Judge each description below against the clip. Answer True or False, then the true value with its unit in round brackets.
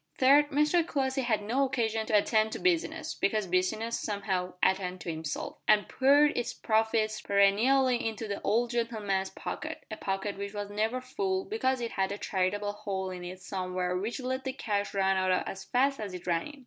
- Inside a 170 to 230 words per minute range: True (190 wpm)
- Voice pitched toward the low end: False (215 Hz)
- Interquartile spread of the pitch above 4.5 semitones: True (5.1 semitones)